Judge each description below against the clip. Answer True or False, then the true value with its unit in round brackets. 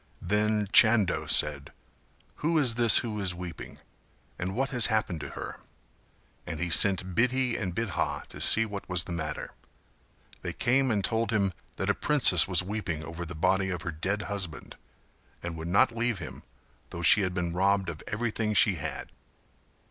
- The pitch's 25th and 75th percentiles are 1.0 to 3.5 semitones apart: False (4.4 semitones)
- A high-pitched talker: False (95 Hz)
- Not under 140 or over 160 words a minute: False (175 wpm)